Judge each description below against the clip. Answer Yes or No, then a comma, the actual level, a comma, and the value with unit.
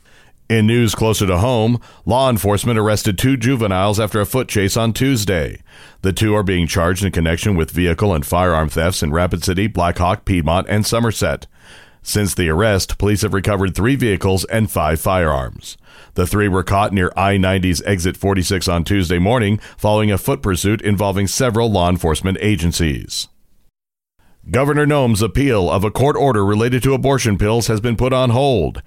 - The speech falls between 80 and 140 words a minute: No, average, 175 wpm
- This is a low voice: Yes, low, 100 Hz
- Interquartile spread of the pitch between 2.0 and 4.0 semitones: Yes, average, 3.7 semitones